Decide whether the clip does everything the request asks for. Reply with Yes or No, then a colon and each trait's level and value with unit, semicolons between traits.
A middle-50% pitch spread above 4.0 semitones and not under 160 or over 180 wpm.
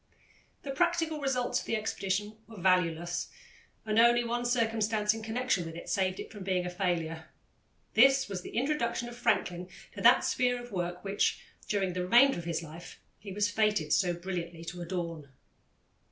Yes: average, 5.2 semitones; average, 175 wpm